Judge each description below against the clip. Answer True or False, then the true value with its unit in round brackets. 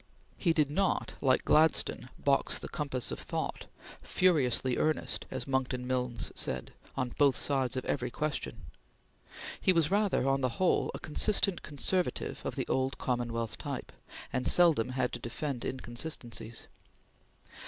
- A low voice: True (130 Hz)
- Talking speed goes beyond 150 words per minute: False (145 wpm)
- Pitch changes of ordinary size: True (3.8 semitones)